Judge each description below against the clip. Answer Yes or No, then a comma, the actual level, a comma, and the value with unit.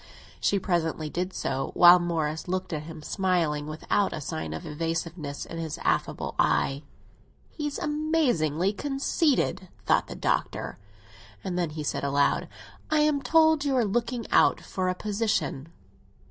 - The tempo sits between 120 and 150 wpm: Yes, average, 145 wpm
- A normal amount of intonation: No, wide, 7.6 semitones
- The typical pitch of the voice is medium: Yes, medium, 175 Hz